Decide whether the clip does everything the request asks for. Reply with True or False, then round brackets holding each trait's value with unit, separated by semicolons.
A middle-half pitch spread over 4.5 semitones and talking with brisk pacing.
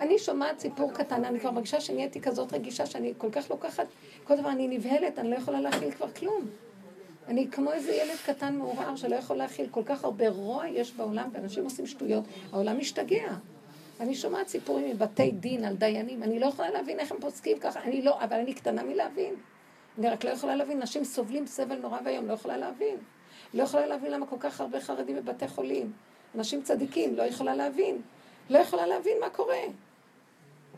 True (4.9 semitones; 160 wpm)